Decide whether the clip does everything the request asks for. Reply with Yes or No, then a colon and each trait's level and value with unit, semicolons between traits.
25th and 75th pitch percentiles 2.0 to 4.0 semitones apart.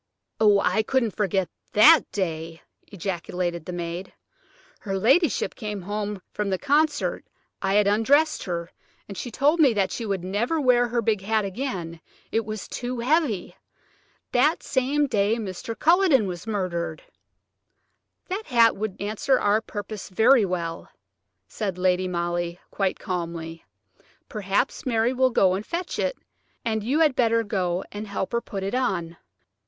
No: average, 4.9 semitones